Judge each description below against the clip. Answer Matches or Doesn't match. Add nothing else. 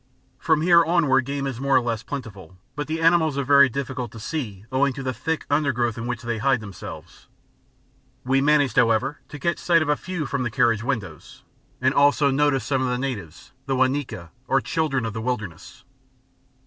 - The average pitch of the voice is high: Doesn't match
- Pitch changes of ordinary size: Matches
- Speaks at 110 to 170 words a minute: Doesn't match